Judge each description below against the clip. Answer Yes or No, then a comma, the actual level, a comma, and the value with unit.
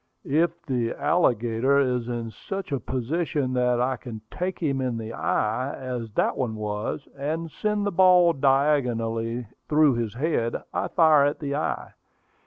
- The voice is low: Yes, low, 130 Hz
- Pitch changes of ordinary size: Yes, average, 4.8 semitones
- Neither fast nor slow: Yes, average, 160 wpm